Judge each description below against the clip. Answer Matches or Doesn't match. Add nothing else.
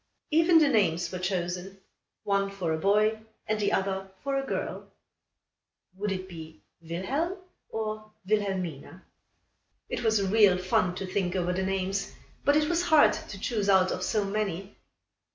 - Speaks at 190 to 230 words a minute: Doesn't match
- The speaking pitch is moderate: Doesn't match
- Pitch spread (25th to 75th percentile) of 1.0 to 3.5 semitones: Matches